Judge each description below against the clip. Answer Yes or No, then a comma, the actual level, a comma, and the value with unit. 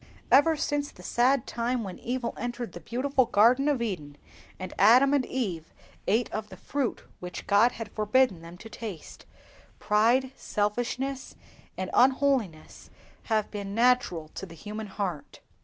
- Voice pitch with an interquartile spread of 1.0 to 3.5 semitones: No, average, 4.5 semitones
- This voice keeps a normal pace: Yes, average, 150 wpm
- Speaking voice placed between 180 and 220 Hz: No, high, 230 Hz